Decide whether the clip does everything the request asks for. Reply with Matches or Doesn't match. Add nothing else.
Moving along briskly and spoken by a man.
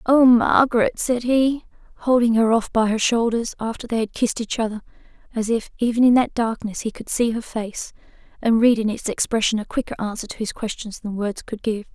Doesn't match